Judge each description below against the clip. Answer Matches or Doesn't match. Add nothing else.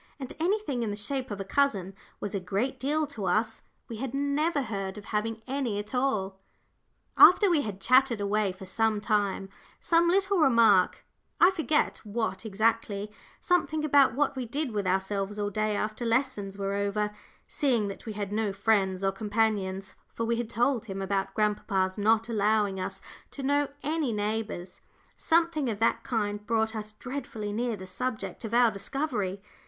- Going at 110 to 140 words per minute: Doesn't match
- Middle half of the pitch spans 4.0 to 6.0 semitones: Matches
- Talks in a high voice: Matches